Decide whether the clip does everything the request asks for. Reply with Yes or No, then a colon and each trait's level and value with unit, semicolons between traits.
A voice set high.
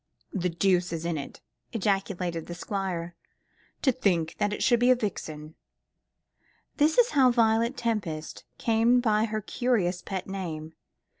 Yes: high, 195 Hz